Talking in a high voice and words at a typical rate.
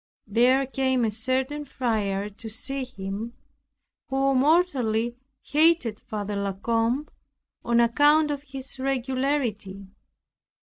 No: very high, 250 Hz; slow, 105 wpm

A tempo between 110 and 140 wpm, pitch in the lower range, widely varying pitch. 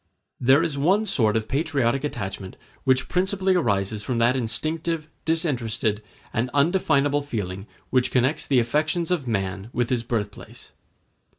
Yes: slow, 135 wpm; low, 130 Hz; wide, 5.7 semitones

